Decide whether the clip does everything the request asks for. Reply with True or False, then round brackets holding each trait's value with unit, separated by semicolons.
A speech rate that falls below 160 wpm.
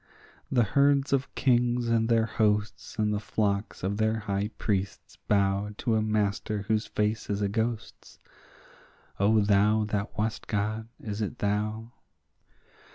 True (145 wpm)